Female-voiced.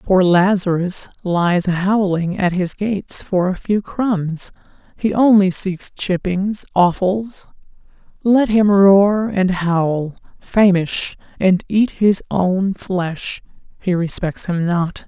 Yes: female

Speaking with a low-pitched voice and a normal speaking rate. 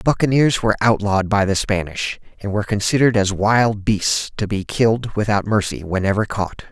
Yes: low, 105 Hz; average, 170 wpm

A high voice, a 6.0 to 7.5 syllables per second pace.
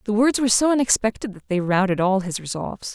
Yes: high, 210 Hz; 6.4 syllables/s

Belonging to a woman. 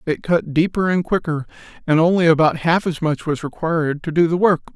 No: male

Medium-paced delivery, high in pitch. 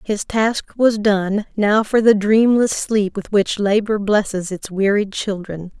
Yes: average, 165 wpm; high, 205 Hz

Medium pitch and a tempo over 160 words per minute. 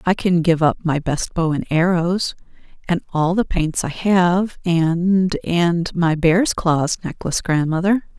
No: medium, 170 Hz; average, 155 wpm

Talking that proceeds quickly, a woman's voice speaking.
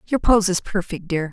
Yes: fast, 225 wpm; female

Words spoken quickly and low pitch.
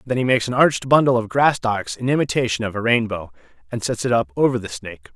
Yes: fast, 245 wpm; low, 115 Hz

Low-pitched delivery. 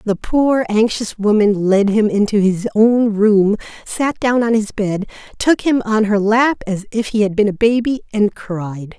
No: high, 215 Hz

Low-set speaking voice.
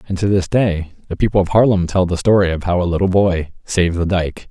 Yes: very low, 90 Hz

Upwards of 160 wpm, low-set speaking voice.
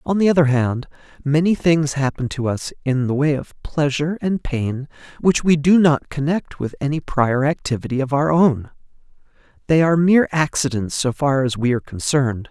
No: average, 180 wpm; medium, 145 Hz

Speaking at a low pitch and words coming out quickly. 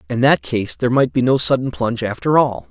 Yes: low, 125 Hz; fast, 245 wpm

